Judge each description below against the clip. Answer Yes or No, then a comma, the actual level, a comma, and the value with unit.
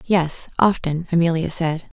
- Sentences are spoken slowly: Yes, slow, 120 wpm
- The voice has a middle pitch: Yes, medium, 165 Hz